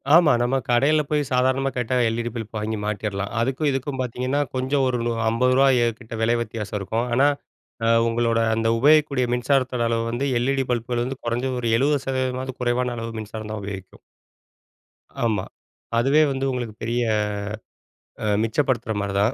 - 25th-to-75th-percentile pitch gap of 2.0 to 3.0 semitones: Yes, narrow, 2.6 semitones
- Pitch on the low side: Yes, low, 120 Hz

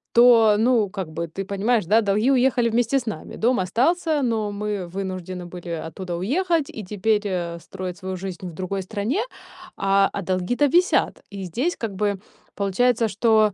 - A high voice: Yes, high, 205 Hz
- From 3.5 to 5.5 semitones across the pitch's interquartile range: Yes, average, 4.3 semitones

